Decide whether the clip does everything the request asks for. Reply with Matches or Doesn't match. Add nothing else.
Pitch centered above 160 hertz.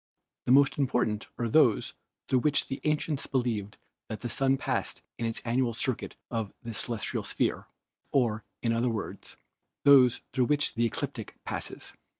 Doesn't match